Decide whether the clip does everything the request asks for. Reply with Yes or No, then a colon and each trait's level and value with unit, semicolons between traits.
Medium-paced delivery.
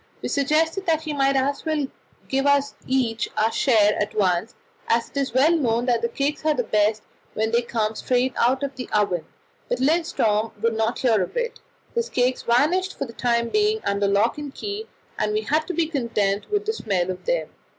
No: fast, 210 wpm